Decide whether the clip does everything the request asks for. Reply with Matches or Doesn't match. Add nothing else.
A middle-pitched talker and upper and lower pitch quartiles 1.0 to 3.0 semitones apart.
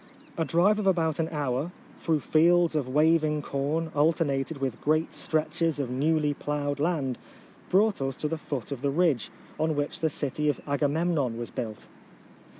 Matches